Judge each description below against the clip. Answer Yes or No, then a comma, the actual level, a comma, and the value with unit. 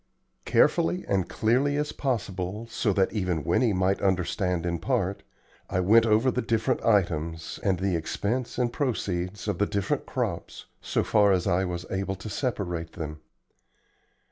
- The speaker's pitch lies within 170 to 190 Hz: No, very low, 95 Hz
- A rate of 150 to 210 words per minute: Yes, average, 155 wpm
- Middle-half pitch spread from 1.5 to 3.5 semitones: No, average, 4.1 semitones